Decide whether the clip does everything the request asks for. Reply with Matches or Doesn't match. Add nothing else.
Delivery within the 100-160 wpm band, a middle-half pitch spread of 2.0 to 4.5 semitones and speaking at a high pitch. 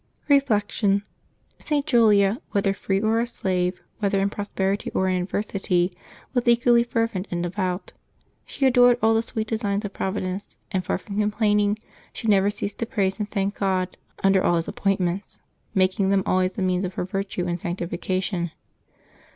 Doesn't match